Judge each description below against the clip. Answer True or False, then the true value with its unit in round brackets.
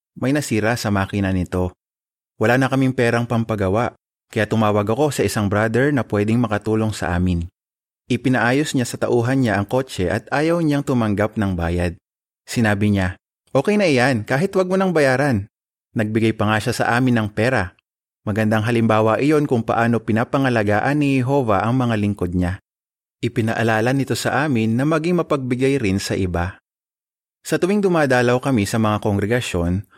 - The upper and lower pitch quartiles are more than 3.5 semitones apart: True (4.0 semitones)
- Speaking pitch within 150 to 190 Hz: False (115 Hz)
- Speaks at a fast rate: True (160 wpm)